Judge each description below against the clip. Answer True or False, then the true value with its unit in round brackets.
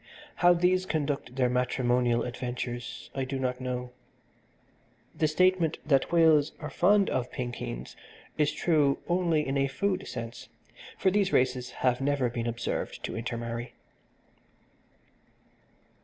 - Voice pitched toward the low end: True (130 Hz)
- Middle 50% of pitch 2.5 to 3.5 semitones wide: False (4.7 semitones)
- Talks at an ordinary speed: False (125 wpm)